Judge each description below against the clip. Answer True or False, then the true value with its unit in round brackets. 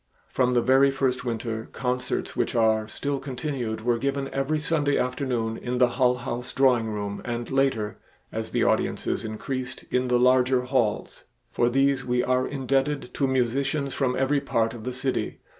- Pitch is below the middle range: True (125 Hz)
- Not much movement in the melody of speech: True (2.2 semitones)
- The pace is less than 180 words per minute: True (170 wpm)